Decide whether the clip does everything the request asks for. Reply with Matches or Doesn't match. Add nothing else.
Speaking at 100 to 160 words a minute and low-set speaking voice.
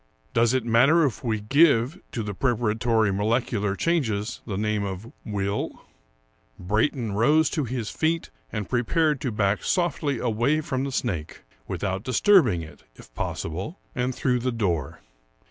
Matches